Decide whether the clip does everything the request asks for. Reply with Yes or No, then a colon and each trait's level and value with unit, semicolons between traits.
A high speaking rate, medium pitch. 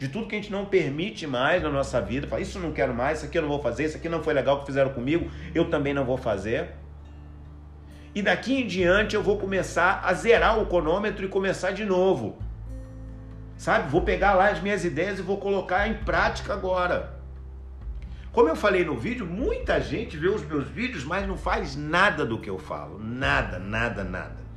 Yes: fast, 210 wpm; medium, 150 Hz